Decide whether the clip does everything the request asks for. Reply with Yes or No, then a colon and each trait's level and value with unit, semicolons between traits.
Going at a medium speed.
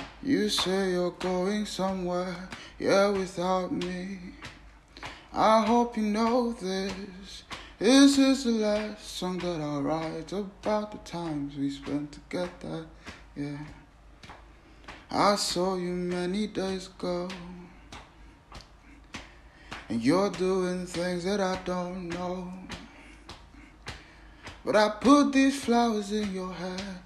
No: slow, 110 wpm